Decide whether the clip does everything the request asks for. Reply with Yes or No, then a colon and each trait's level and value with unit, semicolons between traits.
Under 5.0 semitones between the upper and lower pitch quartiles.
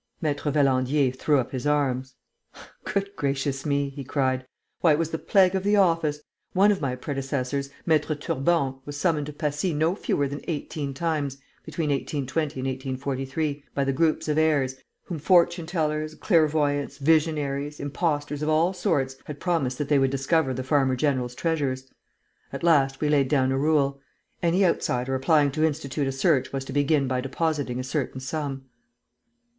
Yes: average, 2.8 semitones